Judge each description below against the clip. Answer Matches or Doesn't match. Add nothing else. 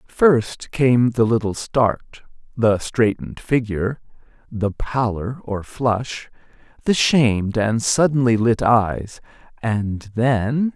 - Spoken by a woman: Doesn't match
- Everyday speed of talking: Doesn't match